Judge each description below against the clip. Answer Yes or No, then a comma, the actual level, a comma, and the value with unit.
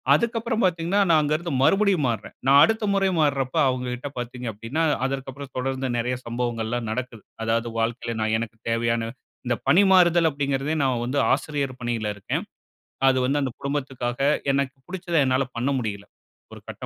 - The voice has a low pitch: Yes, low, 130 Hz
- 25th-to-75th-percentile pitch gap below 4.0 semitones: No, average, 4.4 semitones